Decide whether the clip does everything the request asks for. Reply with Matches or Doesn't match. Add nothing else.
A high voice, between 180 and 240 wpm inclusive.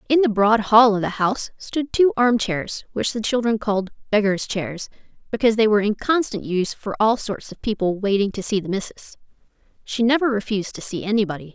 Matches